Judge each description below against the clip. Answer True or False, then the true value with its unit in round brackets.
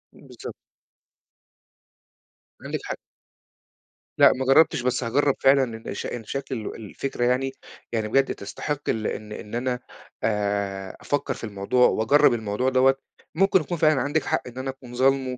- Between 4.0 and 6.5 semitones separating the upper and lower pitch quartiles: False (3.6 semitones)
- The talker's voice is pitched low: True (125 Hz)